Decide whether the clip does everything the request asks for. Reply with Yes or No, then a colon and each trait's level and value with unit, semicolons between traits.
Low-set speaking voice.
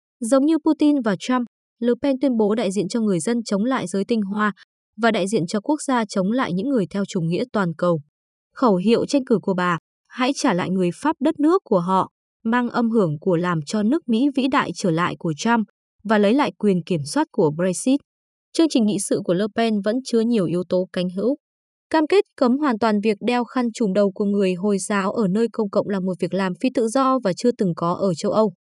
No: high, 220 Hz